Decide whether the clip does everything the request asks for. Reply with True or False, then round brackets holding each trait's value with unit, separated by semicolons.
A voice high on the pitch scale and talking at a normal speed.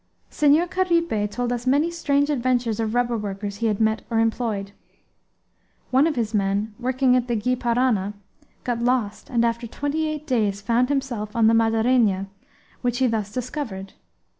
True (235 Hz; 165 wpm)